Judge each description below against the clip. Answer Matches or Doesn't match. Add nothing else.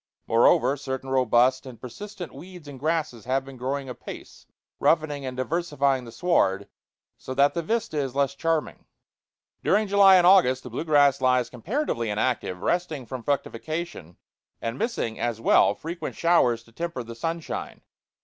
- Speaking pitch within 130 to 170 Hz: Matches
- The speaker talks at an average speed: Matches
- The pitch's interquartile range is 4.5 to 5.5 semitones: Matches